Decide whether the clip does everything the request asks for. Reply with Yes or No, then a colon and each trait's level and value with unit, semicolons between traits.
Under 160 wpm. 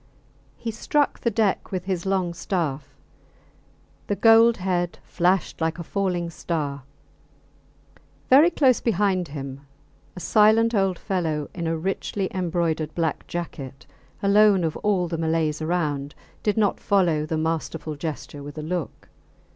Yes: average, 140 wpm